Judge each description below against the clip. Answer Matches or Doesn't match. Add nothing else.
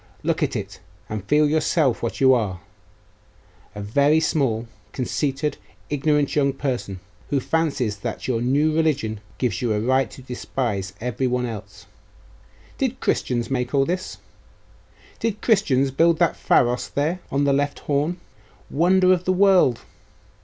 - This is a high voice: Doesn't match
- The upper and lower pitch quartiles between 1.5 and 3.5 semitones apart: Doesn't match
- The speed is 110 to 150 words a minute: Matches